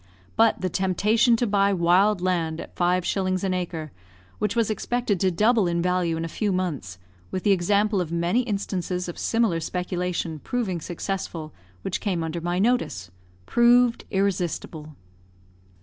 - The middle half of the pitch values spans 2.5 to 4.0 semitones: Yes, average, 3.4 semitones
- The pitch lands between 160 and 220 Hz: Yes, medium, 185 Hz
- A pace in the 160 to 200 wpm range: No, average, 150 wpm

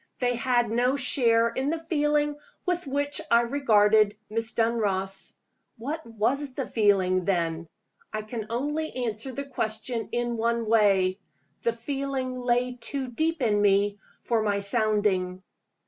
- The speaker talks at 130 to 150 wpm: Yes, average, 140 wpm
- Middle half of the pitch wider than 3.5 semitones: Yes, average, 4.1 semitones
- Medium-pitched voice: No, high, 235 Hz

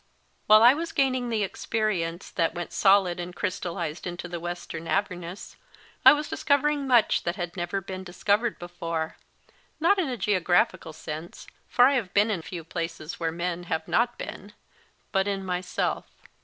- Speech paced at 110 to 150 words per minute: No, average, 180 wpm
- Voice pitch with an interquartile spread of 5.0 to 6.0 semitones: No, average, 4.1 semitones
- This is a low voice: No, medium, 185 Hz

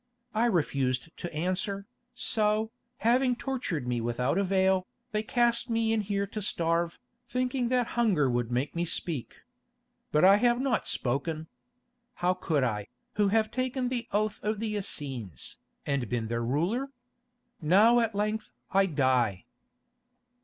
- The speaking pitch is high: Yes, high, 195 Hz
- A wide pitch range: Yes, wide, 8.0 semitones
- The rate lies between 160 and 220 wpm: No, average, 145 wpm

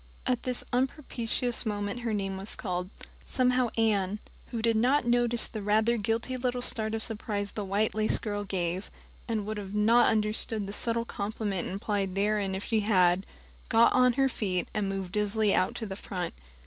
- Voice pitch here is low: No, high, 215 Hz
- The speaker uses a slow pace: No, average, 180 wpm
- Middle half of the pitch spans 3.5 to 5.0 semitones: No, average, 2.8 semitones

